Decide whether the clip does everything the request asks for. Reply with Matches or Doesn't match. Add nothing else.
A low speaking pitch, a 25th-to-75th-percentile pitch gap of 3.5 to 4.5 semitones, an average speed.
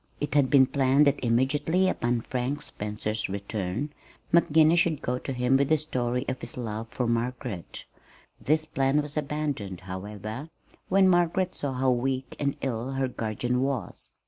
Matches